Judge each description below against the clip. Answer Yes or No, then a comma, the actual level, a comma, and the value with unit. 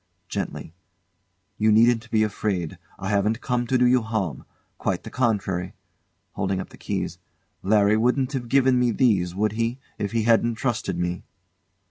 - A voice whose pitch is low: Yes, low, 110 Hz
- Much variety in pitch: No, average, 3.6 semitones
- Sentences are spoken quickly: No, average, 160 wpm